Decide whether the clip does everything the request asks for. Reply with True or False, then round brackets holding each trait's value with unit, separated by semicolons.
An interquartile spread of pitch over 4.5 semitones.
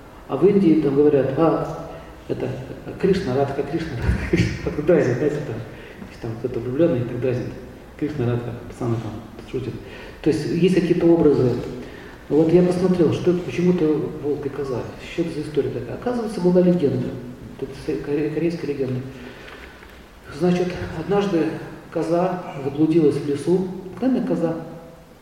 True (5.0 semitones)